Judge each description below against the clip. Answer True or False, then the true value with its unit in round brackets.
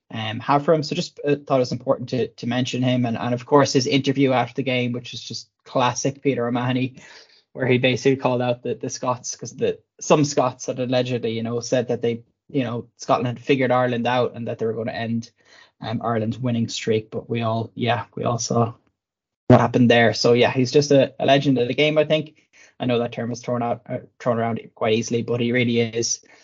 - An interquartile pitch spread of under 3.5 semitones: True (2.5 semitones)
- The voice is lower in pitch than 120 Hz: False (125 Hz)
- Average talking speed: False (240 wpm)